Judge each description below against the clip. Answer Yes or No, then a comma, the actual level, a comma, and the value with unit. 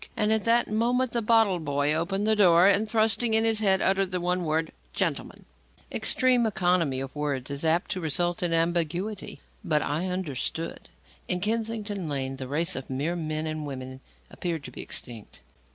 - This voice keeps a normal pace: Yes, average, 180 wpm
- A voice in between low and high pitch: Yes, medium, 175 Hz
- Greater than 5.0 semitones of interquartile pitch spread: Yes, wide, 5.6 semitones